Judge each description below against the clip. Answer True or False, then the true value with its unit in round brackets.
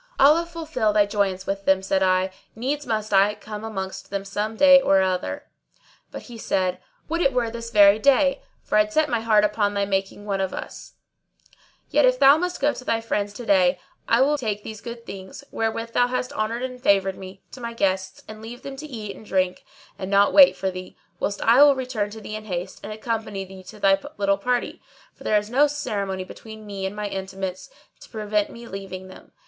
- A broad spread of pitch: False (3.6 semitones)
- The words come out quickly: True (220 wpm)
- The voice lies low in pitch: False (210 Hz)